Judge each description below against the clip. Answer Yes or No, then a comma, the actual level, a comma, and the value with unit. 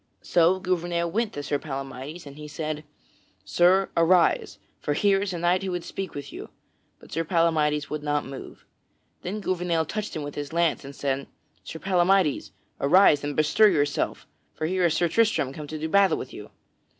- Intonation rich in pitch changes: No, average, 3.8 semitones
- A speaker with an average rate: Yes, average, 185 wpm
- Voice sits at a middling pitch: Yes, medium, 165 Hz